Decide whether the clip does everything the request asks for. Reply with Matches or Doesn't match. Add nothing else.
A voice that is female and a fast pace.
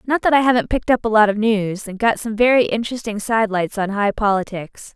Matches